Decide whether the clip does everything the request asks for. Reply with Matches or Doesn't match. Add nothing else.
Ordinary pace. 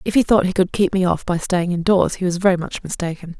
Doesn't match